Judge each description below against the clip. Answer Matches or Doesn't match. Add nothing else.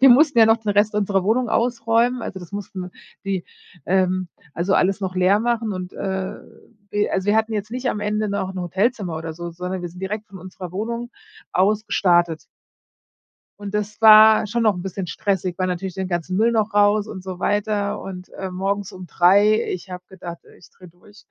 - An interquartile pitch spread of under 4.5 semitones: Matches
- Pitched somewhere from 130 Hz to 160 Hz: Doesn't match